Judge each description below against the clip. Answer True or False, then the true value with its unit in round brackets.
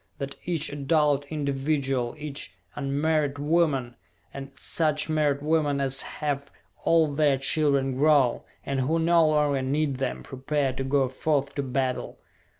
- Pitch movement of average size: False (2.1 semitones)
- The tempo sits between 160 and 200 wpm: False (140 wpm)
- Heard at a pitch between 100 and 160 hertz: True (140 Hz)